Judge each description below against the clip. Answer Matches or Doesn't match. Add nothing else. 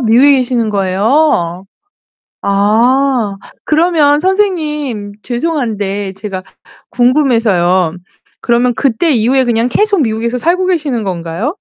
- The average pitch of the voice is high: Matches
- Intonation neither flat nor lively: Doesn't match